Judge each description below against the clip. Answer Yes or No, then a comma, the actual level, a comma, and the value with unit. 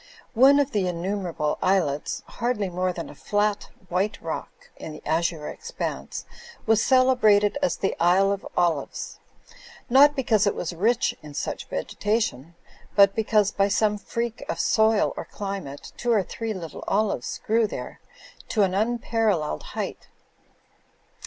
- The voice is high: Yes, high, 205 Hz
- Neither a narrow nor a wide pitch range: Yes, average, 4.2 semitones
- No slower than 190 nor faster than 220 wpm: No, average, 145 wpm